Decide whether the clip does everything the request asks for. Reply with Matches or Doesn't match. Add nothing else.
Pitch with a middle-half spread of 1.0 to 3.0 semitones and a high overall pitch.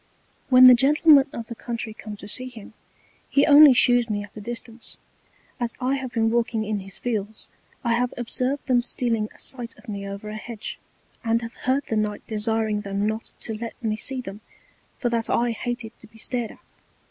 Matches